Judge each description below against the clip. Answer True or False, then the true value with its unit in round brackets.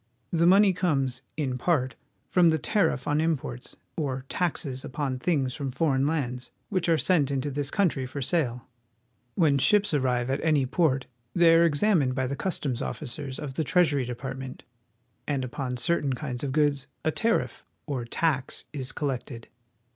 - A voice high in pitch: False (140 Hz)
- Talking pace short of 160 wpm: False (165 wpm)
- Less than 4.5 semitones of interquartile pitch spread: True (4.1 semitones)